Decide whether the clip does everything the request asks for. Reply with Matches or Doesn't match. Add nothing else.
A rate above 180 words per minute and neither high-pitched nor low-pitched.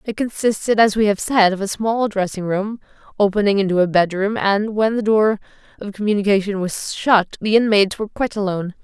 Doesn't match